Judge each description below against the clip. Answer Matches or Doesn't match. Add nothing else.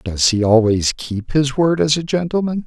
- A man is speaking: Matches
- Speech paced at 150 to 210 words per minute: Matches